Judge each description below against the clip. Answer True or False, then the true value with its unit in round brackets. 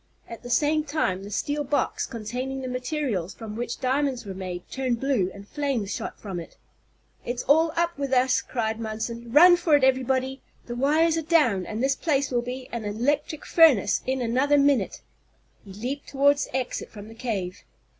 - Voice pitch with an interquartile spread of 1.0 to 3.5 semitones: False (4.3 semitones)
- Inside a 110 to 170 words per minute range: False (185 wpm)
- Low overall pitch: False (255 Hz)